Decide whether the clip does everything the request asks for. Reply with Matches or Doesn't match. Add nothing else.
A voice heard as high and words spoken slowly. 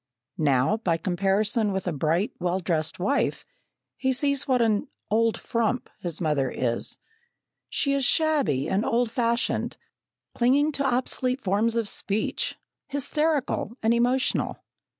Matches